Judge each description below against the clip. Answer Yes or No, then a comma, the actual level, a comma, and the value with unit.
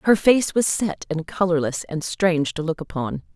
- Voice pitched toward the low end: No, medium, 170 Hz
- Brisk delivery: No, average, 195 wpm